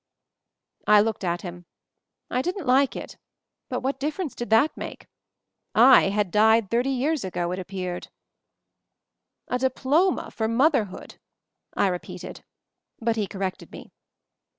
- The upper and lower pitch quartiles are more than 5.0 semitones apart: Yes, wide, 5.6 semitones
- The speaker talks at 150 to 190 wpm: No, slow, 135 wpm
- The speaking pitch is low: No, high, 225 Hz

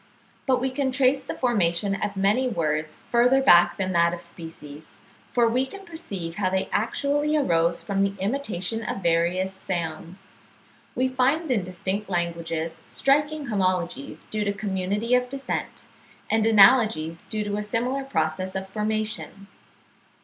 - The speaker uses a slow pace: No, average, 150 wpm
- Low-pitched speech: No, high, 200 Hz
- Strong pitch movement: Yes, wide, 6.3 semitones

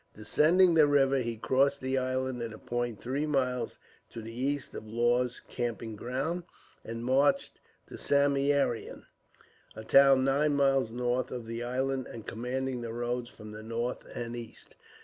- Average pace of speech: Yes, average, 160 wpm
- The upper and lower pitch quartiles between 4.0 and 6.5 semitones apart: No, narrow, 2.6 semitones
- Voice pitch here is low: Yes, low, 125 Hz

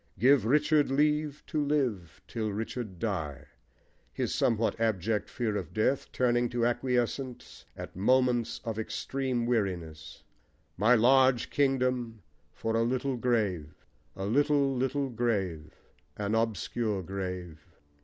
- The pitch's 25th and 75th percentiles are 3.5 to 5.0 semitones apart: Yes, average, 4.4 semitones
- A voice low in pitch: Yes, low, 115 Hz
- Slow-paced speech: Yes, slow, 120 wpm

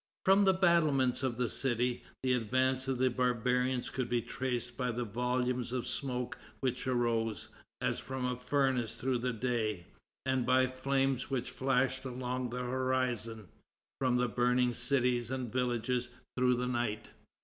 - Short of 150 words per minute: No, average, 160 wpm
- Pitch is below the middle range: Yes, low, 125 Hz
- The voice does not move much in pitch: Yes, narrow, 1.2 semitones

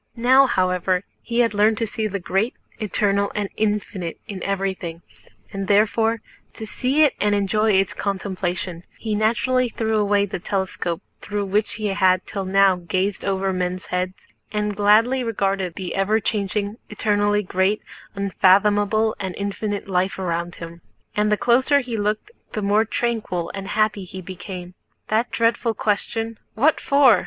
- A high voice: Yes, high, 205 Hz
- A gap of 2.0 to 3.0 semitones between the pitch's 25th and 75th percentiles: Yes, narrow, 2.5 semitones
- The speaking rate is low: No, average, 150 wpm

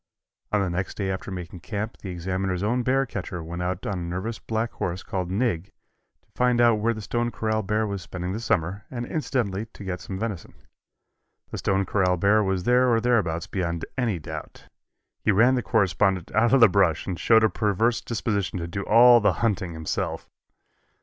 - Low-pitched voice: Yes, low, 100 Hz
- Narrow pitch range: No, average, 3.9 semitones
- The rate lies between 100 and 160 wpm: No, average, 195 wpm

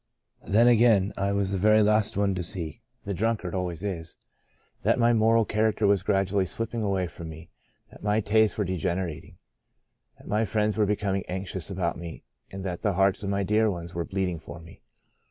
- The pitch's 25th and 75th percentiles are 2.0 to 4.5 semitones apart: Yes, average, 2.8 semitones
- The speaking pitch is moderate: No, low, 100 Hz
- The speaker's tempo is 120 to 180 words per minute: No, average, 190 wpm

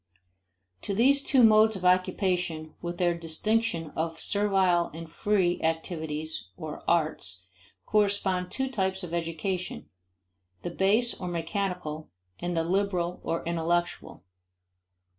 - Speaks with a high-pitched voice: No, medium, 175 Hz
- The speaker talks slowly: Yes, slow, 120 wpm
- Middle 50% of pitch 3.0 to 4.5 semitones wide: Yes, average, 3.4 semitones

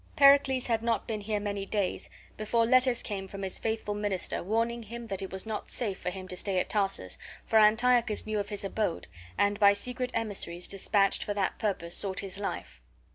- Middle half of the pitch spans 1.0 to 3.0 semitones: Yes, average, 2.7 semitones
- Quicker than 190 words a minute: Yes, average, 200 wpm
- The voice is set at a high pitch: Yes, high, 205 Hz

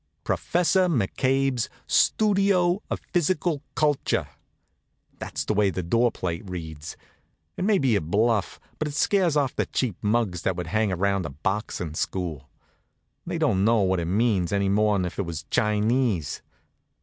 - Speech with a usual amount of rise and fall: No, wide, 7.0 semitones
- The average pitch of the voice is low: Yes, low, 105 Hz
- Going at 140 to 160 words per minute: Yes, average, 155 wpm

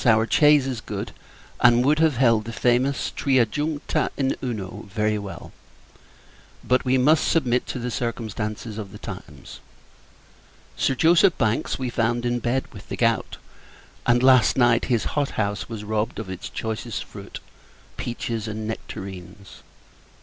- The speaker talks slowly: No, average, 150 wpm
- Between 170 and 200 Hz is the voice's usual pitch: No, low, 120 Hz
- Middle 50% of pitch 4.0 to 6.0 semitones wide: No, average, 3.2 semitones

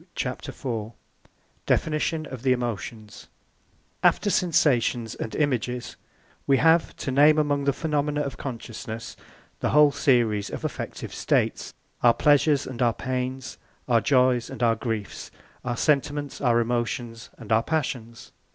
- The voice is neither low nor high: No, low, 125 Hz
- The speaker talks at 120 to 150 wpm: Yes, average, 140 wpm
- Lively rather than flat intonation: No, average, 3.7 semitones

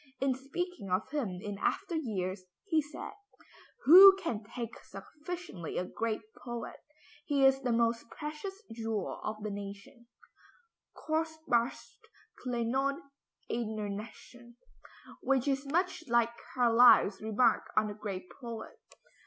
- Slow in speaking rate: Yes, slow, 120 wpm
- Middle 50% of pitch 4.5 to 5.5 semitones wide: Yes, average, 5.1 semitones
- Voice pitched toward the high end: Yes, high, 240 Hz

